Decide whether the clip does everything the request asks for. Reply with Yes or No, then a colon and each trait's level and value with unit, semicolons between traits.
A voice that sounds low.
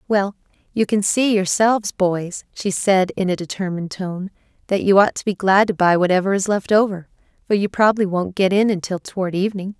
No: high, 195 Hz